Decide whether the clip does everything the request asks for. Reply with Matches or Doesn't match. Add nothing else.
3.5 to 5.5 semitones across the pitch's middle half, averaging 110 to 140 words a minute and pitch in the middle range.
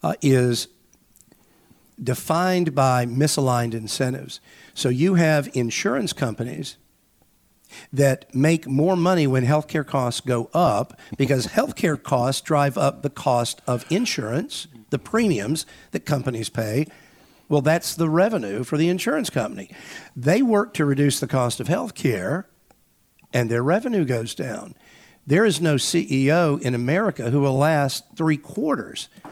Matches